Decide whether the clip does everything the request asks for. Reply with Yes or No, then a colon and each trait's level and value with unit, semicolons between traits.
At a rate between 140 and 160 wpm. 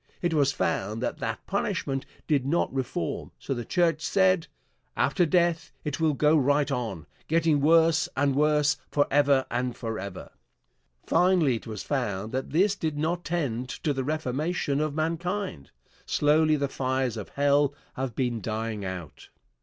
Yes: average, 155 wpm